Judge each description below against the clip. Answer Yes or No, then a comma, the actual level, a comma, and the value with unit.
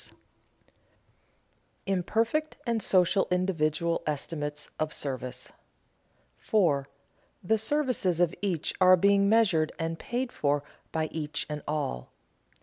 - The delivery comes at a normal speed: No, slow, 110 wpm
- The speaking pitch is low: No, medium, 170 Hz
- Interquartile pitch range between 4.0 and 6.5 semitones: Yes, average, 4.8 semitones